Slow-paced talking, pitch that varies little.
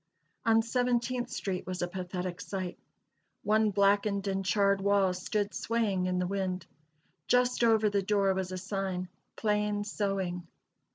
No: average, 145 wpm; narrow, 2.3 semitones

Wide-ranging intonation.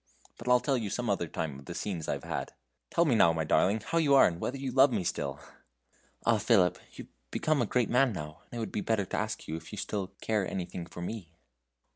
Yes: wide, 6.1 semitones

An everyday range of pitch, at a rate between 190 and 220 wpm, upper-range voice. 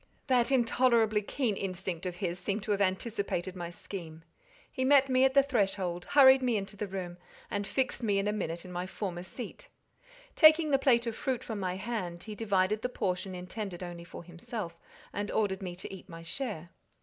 Yes: average, 4.8 semitones; average, 195 wpm; high, 200 Hz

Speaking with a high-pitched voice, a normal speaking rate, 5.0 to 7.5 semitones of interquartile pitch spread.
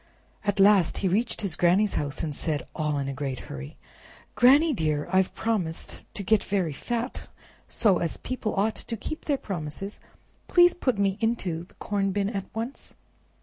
Yes: high, 195 Hz; average, 175 wpm; wide, 5.5 semitones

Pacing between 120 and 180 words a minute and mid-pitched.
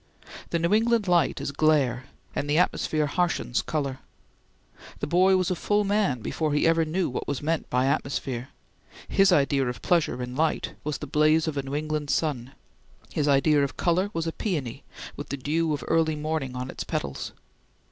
No: average, 190 wpm; medium, 155 Hz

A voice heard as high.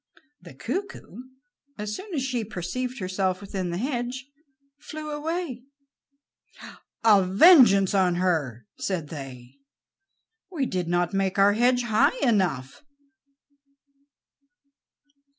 Yes: high, 200 Hz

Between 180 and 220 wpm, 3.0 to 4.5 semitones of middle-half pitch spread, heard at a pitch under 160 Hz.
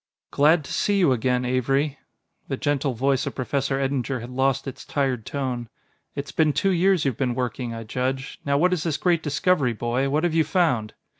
Yes: average, 200 wpm; average, 3.3 semitones; low, 135 Hz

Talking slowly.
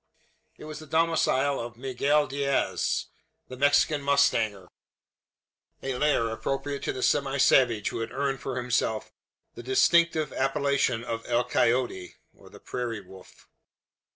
Yes: slow, 125 wpm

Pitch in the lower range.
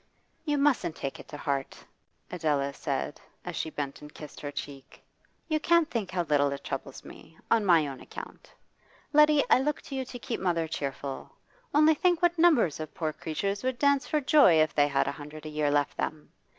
No: medium, 160 Hz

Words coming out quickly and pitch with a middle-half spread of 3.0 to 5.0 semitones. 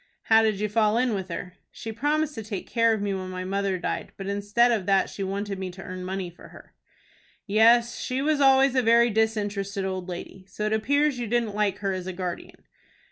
Yes: fast, 225 wpm; average, 3.4 semitones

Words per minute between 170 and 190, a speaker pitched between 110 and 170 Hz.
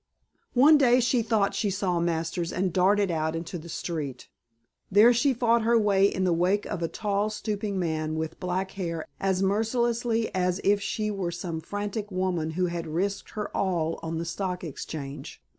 No: average, 180 wpm; high, 190 Hz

